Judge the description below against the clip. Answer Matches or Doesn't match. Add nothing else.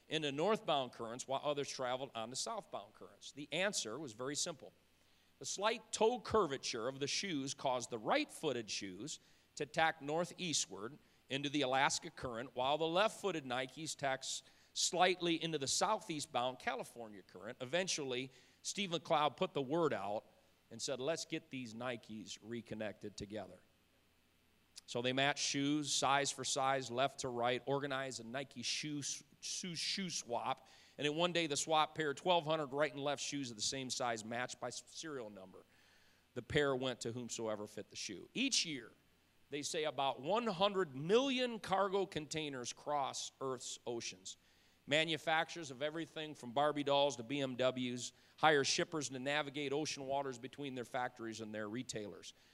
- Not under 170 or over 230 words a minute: Doesn't match